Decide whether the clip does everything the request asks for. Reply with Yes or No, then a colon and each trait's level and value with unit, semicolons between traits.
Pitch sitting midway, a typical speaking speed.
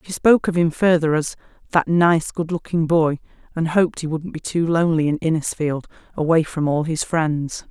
Yes: medium, 160 Hz; average, 195 wpm